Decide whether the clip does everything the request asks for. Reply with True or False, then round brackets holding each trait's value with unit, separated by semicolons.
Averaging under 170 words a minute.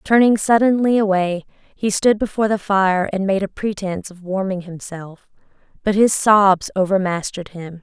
True (155 wpm)